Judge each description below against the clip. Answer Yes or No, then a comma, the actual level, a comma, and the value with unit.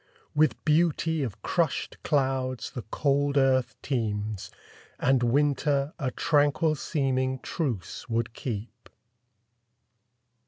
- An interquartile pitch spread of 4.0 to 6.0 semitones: No, average, 3.4 semitones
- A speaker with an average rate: No, slow, 95 wpm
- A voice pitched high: No, low, 135 Hz